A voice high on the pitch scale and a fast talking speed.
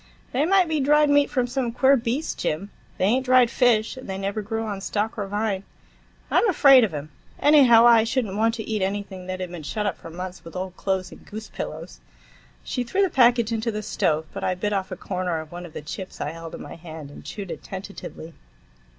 Yes: high, 210 Hz; fast, 235 wpm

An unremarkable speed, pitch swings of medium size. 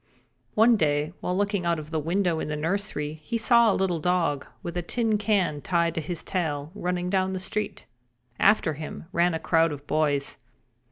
Yes: average, 190 wpm; average, 4.1 semitones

